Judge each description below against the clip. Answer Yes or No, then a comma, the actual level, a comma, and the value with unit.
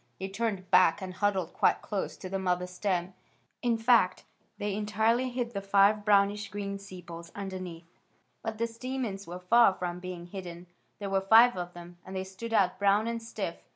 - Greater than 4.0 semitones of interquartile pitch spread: No, average, 3.0 semitones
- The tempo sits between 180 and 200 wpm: Yes, average, 185 wpm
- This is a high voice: Yes, high, 195 Hz